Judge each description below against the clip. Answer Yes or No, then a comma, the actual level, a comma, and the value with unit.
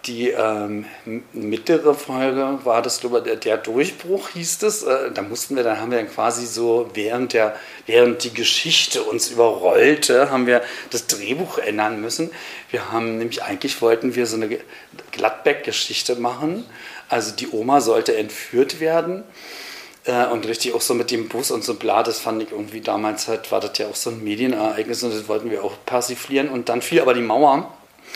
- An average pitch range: No, wide, 6.4 semitones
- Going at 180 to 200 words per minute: Yes, average, 185 wpm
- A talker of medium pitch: No, low, 120 Hz